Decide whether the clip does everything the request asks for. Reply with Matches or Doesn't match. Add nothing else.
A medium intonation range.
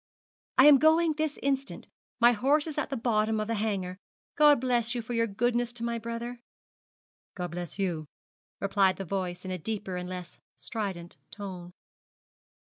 Matches